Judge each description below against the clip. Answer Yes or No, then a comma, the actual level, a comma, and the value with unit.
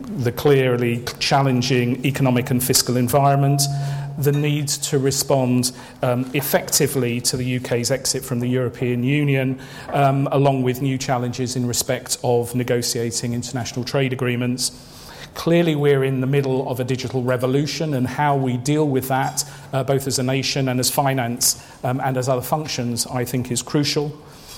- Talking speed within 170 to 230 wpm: No, average, 160 wpm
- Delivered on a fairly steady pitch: Yes, narrow, 2.0 semitones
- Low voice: Yes, low, 130 Hz